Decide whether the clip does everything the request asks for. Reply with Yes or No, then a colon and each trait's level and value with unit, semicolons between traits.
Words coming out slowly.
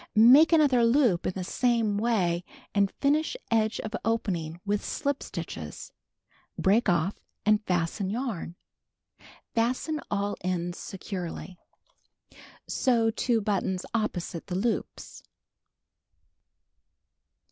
Yes: slow, 105 wpm